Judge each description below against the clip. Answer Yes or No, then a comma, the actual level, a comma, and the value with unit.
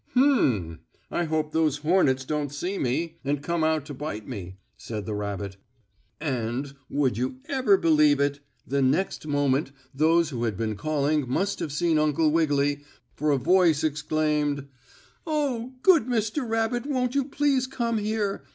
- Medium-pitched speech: Yes, medium, 155 Hz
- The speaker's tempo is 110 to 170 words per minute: Yes, average, 160 wpm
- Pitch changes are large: Yes, wide, 6.3 semitones